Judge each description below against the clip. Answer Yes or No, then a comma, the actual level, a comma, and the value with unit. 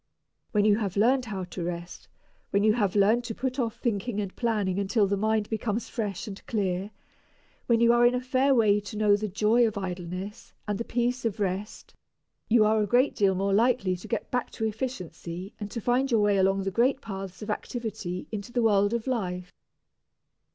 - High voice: Yes, high, 210 Hz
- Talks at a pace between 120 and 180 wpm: No, fast, 205 wpm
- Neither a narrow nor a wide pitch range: Yes, average, 3.2 semitones